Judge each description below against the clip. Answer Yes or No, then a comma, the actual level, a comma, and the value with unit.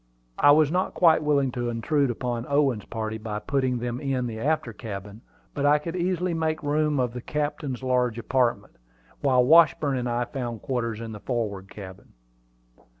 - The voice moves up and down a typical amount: Yes, average, 4.1 semitones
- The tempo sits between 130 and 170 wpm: No, average, 180 wpm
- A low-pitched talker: Yes, low, 125 Hz